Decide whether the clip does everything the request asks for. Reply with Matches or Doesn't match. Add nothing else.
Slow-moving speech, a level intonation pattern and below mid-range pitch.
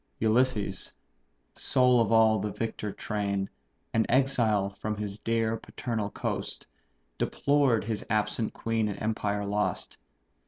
Matches